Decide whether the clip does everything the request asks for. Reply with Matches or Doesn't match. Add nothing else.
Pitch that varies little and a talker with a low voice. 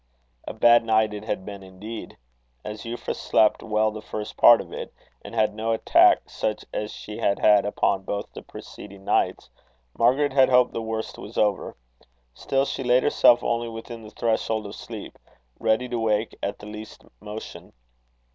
Matches